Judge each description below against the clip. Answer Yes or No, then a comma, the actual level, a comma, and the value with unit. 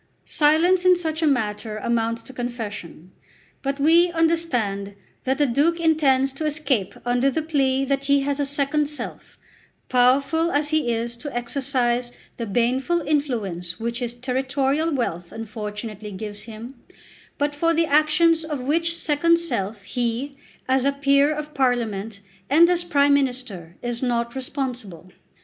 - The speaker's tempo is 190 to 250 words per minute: No, average, 150 wpm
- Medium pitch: No, very high, 265 Hz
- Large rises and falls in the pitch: No, average, 4.4 semitones